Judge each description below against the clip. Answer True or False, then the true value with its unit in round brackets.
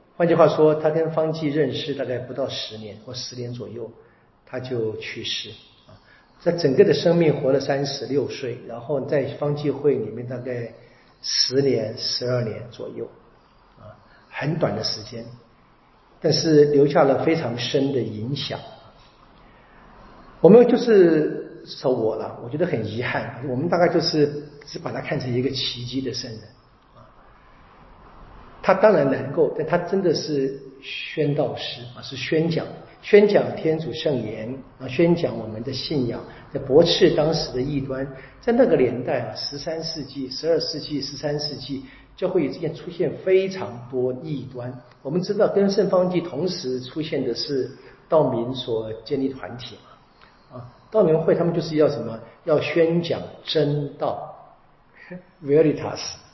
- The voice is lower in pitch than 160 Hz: True (140 Hz)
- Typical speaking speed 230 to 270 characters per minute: True (240 characters per minute)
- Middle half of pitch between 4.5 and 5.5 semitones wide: False (4.1 semitones)